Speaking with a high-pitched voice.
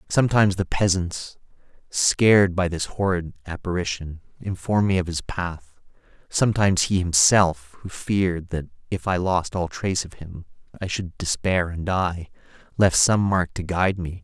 No: very low, 90 Hz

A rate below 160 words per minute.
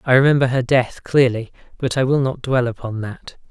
No: fast, 205 wpm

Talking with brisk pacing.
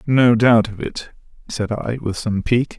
No: average, 195 wpm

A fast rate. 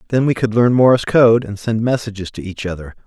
Yes: fast, 235 wpm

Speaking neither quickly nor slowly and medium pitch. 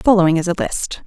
No: fast, 225 wpm; medium, 180 Hz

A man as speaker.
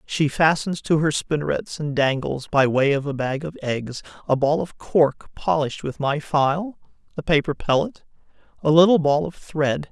Yes: male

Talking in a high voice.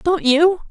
Yes: very high, 325 Hz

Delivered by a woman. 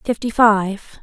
Yes: female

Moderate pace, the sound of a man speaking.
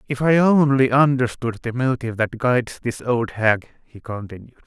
Yes: average, 165 wpm; male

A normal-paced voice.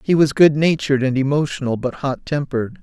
Yes: average, 170 wpm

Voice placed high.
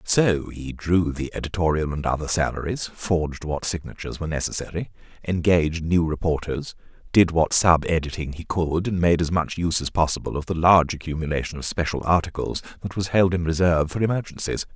No: very low, 85 Hz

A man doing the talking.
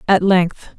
No: female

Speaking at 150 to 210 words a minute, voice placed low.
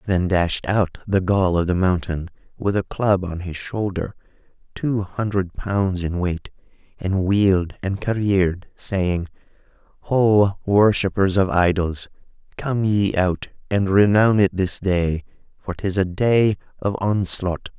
No: average, 140 wpm; very low, 95 Hz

